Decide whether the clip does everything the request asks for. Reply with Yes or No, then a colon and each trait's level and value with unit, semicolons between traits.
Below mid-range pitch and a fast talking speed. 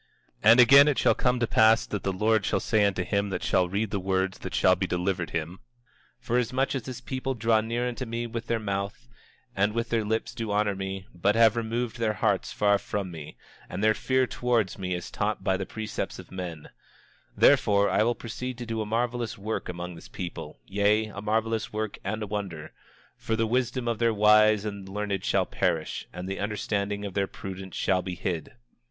Yes: low, 105 Hz; fast, 215 wpm